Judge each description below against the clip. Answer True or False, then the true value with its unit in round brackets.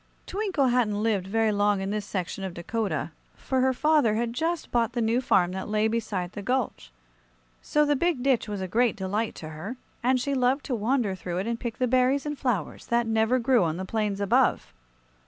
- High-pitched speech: True (225 Hz)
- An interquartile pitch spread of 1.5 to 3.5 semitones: False (4.1 semitones)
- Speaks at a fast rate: True (210 wpm)